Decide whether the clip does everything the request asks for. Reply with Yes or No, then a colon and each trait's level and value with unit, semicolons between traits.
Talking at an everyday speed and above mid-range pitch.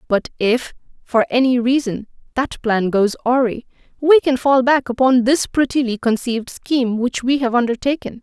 Yes: average, 160 wpm; very high, 250 Hz